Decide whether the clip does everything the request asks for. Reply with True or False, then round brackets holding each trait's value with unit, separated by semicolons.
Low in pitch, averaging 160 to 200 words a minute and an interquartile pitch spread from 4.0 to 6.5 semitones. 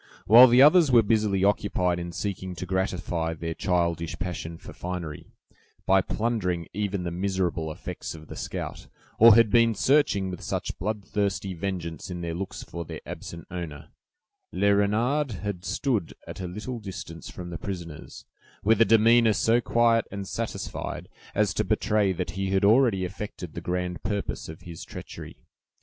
False (95 Hz; 165 wpm; 3.6 semitones)